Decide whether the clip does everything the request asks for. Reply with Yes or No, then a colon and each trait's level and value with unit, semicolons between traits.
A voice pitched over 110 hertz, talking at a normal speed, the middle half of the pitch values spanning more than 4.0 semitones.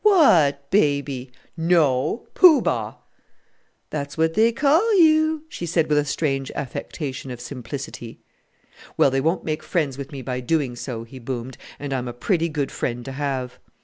Yes: medium, 140 Hz; average, 165 wpm; average, 4.7 semitones